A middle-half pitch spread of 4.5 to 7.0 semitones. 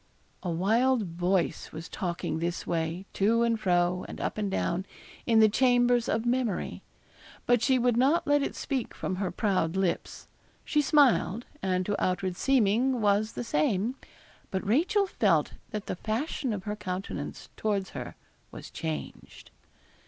Yes: average, 5.0 semitones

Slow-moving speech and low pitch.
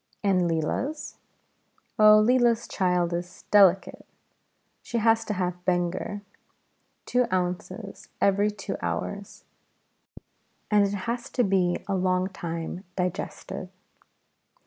No: slow, 105 wpm; high, 195 Hz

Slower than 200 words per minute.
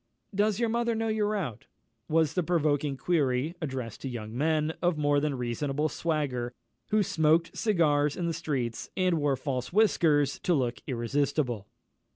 Yes: average, 160 wpm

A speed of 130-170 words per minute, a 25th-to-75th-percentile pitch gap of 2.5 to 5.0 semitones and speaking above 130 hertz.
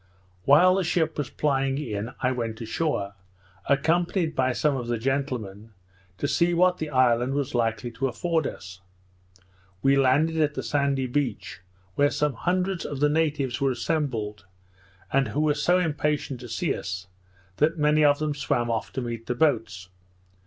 Yes: average, 165 wpm; average, 4.3 semitones; medium, 140 Hz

